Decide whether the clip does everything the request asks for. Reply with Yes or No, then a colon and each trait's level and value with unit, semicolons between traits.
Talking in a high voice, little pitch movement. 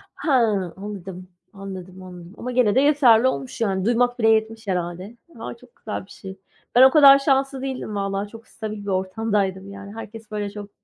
No: high, 210 Hz; average, 3.8 semitones